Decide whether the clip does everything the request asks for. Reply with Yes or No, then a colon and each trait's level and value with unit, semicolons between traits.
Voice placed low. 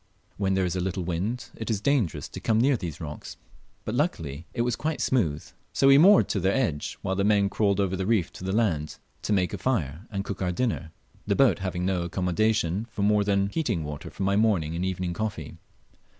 Yes: low, 100 Hz